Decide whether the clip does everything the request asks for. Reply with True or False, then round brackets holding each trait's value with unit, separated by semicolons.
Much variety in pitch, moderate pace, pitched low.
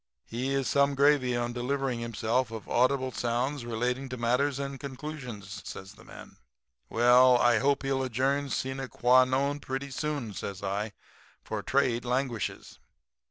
False (2.4 semitones; 150 wpm; 130 Hz)